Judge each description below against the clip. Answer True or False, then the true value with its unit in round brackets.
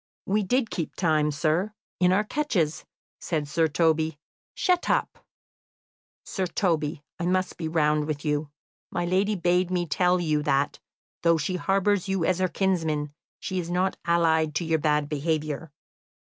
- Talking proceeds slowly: False (160 wpm)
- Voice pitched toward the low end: False (170 Hz)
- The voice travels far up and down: False (3.4 semitones)